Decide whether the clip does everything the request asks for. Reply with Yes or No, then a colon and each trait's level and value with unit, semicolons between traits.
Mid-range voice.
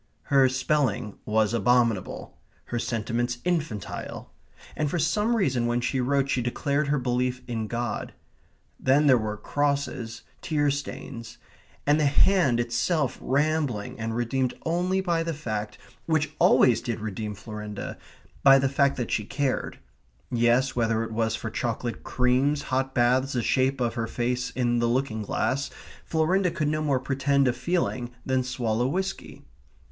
No: low, 130 Hz